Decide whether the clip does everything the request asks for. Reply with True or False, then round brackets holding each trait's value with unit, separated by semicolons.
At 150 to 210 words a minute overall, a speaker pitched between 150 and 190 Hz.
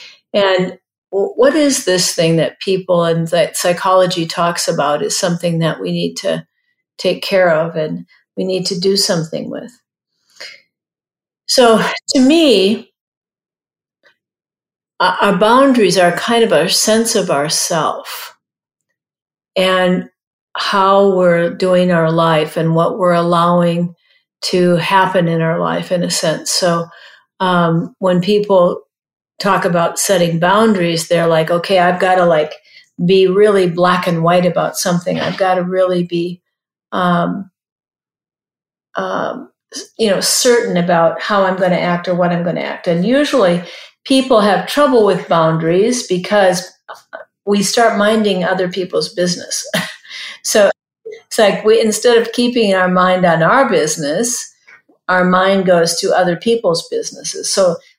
False (140 wpm; 185 Hz)